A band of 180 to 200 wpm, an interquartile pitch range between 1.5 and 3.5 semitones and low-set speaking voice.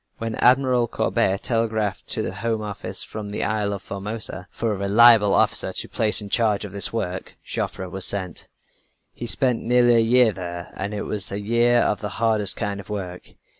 Yes: average, 195 wpm; narrow, 2.6 semitones; low, 105 Hz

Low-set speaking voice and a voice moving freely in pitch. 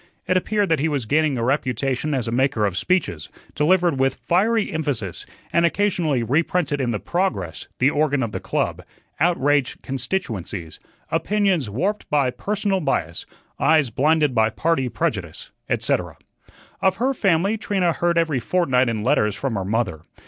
No: medium, 145 Hz; wide, 6.7 semitones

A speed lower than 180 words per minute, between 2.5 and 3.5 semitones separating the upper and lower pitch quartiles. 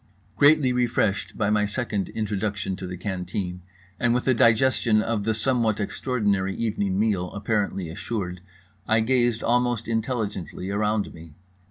Yes: average, 140 wpm; average, 3.1 semitones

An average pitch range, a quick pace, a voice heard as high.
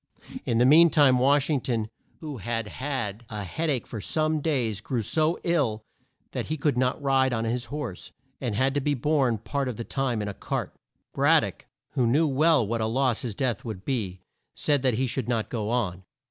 No: average, 4.1 semitones; fast, 215 wpm; low, 125 Hz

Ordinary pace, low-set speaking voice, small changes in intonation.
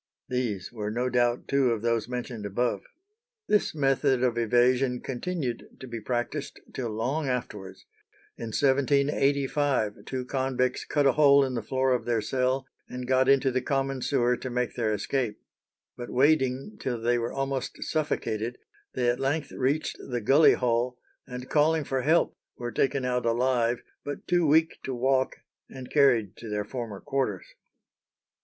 Yes: average, 160 wpm; low, 125 Hz; narrow, 2.2 semitones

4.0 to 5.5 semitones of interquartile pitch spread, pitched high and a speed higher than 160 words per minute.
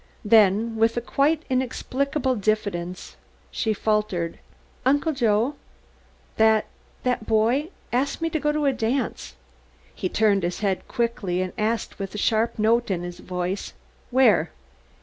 No: average, 4.4 semitones; high, 220 Hz; average, 140 wpm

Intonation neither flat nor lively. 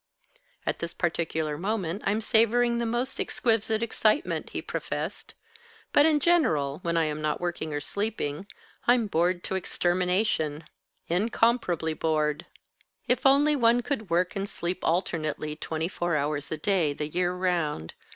No: wide, 6.2 semitones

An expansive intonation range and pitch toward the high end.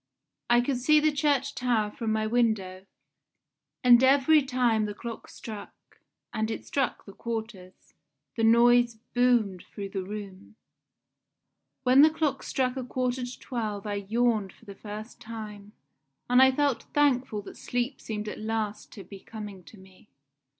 No: average, 3.2 semitones; high, 230 Hz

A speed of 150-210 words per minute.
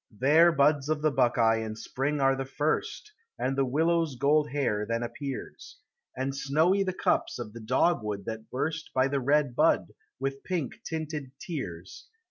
Yes: average, 165 wpm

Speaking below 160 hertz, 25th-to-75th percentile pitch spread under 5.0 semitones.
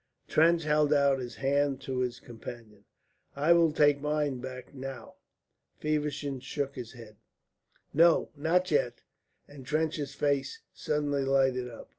Yes: medium, 140 Hz; narrow, 2.6 semitones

